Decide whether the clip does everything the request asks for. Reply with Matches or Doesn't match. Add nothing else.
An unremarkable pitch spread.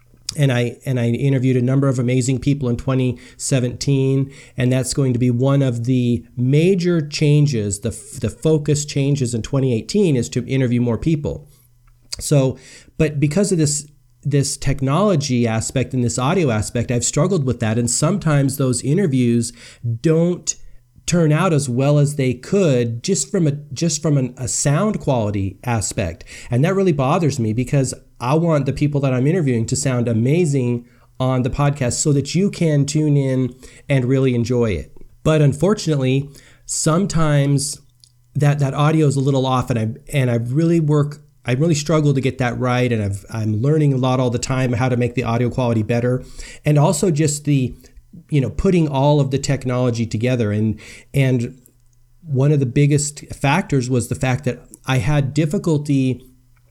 Matches